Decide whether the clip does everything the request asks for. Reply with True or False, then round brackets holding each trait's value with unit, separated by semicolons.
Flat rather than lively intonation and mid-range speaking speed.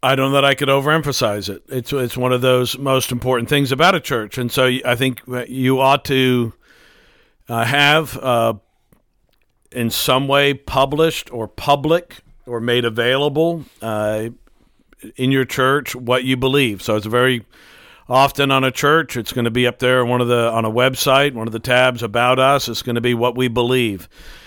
True (2.2 semitones; 190 wpm)